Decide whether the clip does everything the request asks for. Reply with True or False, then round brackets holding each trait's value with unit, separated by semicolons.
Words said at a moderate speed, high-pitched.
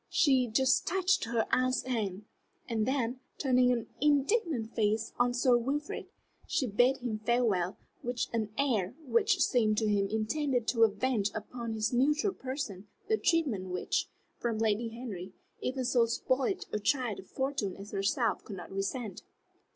True (155 wpm; 240 Hz)